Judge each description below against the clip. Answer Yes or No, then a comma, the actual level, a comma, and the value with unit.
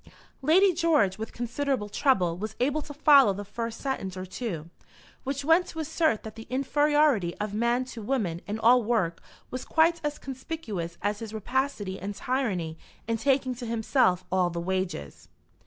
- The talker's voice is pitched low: No, high, 230 Hz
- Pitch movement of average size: No, wide, 6.1 semitones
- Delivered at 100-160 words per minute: No, average, 170 wpm